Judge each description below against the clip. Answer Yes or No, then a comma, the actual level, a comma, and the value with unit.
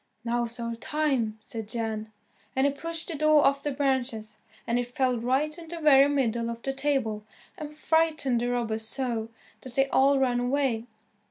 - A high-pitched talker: Yes, very high, 260 Hz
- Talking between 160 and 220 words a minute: Yes, average, 180 wpm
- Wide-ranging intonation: No, average, 3.6 semitones